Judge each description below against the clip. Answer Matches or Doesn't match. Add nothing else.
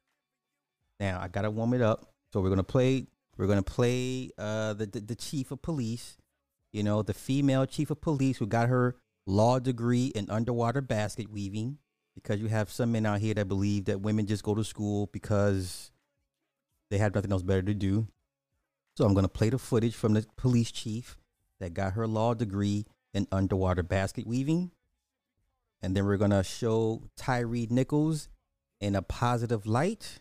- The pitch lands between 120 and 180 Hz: Doesn't match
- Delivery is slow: Doesn't match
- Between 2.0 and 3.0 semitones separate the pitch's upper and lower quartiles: Doesn't match